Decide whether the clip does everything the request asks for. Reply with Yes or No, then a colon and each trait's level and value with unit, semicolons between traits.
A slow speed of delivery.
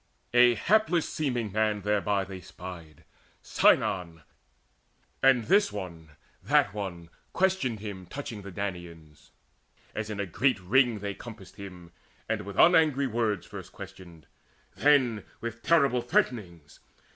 Yes: slow, 125 wpm